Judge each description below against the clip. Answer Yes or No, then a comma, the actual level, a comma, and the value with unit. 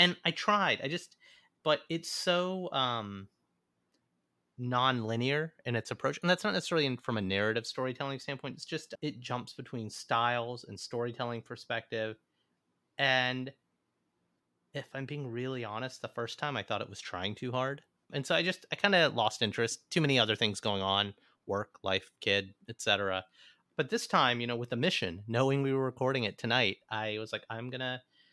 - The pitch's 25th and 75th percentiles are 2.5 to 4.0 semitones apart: No, average, 4.4 semitones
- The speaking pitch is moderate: No, low, 125 Hz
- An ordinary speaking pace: Yes, average, 180 wpm